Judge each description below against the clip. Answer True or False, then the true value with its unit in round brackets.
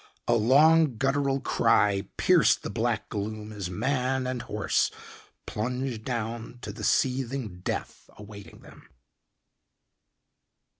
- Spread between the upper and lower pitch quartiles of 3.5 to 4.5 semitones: True (4.0 semitones)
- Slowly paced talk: True (110 wpm)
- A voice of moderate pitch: False (120 Hz)